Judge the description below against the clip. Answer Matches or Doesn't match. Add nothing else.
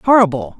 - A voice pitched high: Matches